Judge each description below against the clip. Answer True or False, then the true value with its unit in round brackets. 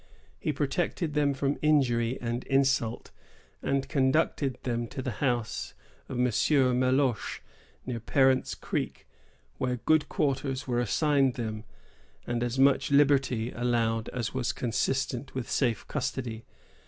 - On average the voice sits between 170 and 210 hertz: False (130 Hz)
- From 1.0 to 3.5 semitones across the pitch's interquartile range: True (2.5 semitones)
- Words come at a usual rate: False (130 wpm)